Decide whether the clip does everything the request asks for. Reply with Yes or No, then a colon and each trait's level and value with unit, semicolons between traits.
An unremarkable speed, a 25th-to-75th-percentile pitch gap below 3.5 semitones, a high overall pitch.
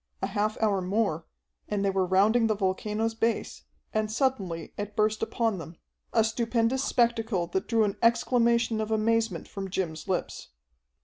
Yes: average, 160 wpm; average, 2.9 semitones; high, 215 Hz